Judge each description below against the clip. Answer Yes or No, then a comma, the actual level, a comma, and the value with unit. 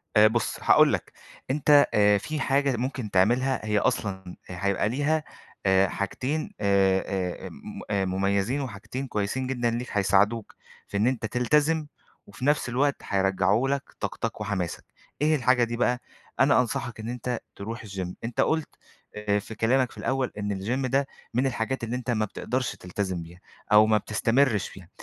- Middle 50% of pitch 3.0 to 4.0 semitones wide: No, average, 4.5 semitones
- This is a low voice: Yes, low, 115 Hz